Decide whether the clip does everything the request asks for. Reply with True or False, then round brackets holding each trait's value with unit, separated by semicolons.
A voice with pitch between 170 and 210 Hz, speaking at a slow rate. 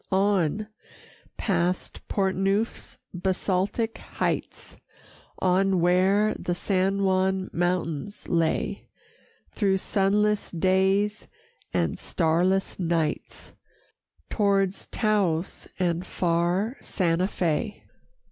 True (190 Hz; 80 wpm)